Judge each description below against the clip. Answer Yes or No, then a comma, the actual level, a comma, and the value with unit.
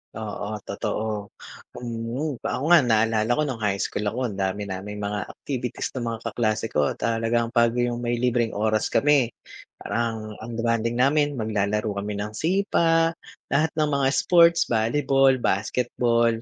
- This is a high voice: No, low, 115 Hz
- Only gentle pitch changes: No, average, 3.2 semitones